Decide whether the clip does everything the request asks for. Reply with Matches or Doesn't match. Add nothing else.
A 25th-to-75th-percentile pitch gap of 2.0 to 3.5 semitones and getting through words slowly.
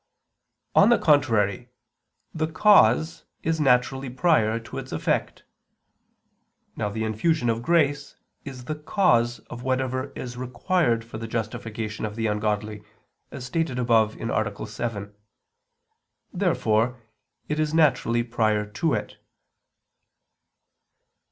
Doesn't match